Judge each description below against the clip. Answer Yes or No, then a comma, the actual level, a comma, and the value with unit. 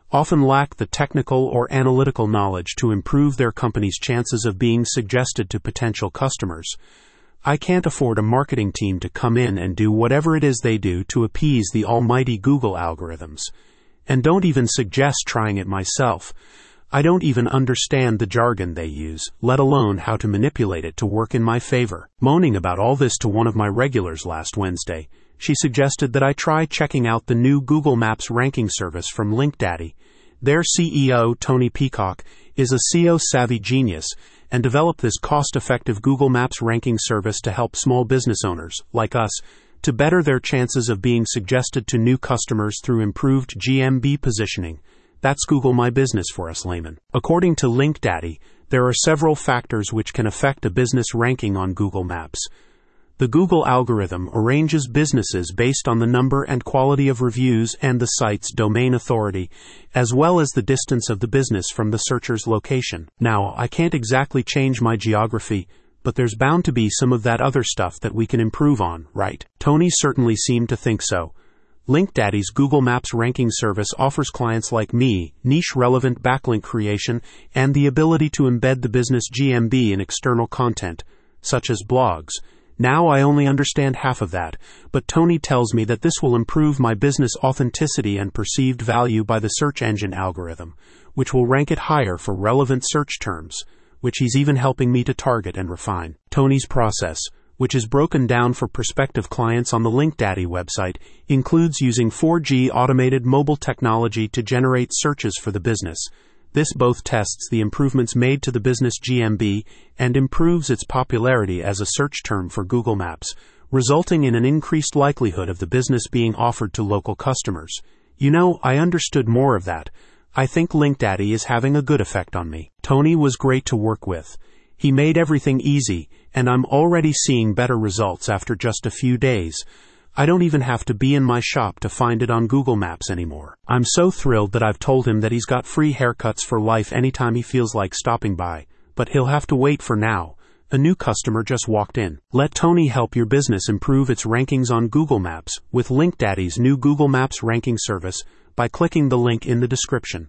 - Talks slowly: No, average, 180 wpm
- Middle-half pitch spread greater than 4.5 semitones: No, average, 4.0 semitones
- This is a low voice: Yes, low, 125 Hz